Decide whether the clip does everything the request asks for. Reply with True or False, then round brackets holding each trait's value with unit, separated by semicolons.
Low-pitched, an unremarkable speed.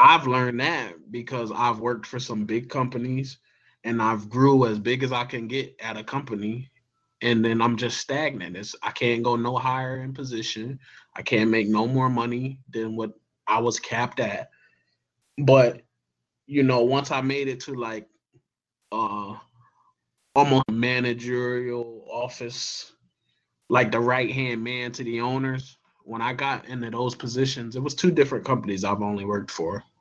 True (120 Hz; 165 wpm)